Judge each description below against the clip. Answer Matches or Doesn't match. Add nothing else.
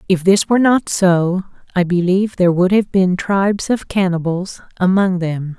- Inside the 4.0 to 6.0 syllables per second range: Matches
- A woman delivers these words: Matches